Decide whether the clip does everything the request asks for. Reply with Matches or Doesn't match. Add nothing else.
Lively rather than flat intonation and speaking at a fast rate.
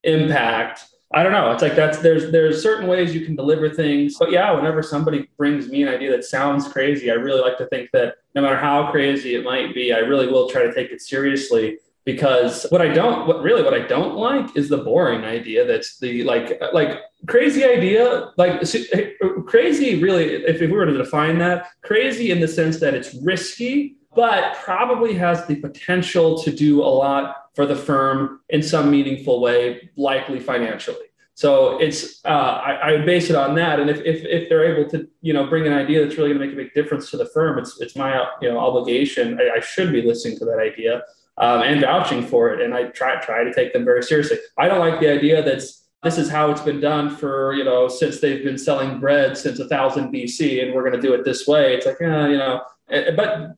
Matches